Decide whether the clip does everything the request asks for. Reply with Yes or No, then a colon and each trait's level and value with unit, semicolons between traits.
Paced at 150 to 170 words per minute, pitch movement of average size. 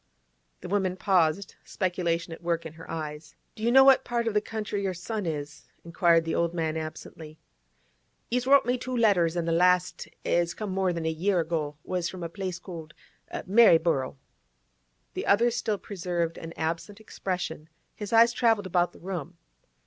No: average, 180 wpm; average, 3.9 semitones